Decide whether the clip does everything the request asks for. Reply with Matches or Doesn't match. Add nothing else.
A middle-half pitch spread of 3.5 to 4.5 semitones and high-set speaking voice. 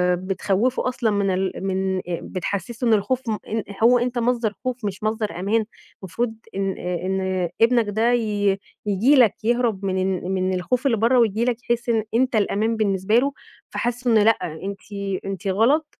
Matches